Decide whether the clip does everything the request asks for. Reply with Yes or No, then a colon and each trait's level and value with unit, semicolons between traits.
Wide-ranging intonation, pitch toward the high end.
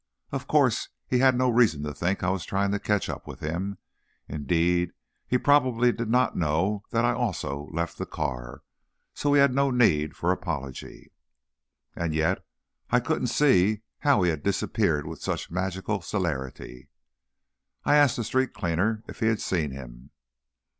No: wide, 7.5 semitones; very low, 95 Hz